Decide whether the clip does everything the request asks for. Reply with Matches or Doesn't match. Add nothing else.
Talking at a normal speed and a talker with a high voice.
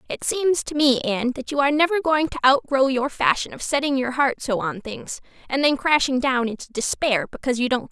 Doesn't match